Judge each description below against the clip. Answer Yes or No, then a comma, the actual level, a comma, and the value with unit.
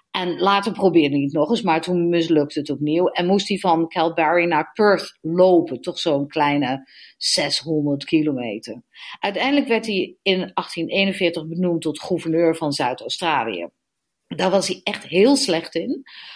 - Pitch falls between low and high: Yes, medium, 170 Hz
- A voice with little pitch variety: No, average, 3.8 semitones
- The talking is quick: No, average, 160 wpm